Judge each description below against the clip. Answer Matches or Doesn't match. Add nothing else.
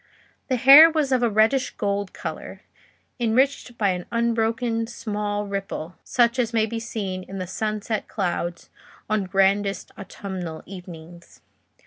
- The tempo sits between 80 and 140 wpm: Matches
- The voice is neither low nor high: Doesn't match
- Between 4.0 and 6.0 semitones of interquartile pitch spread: Doesn't match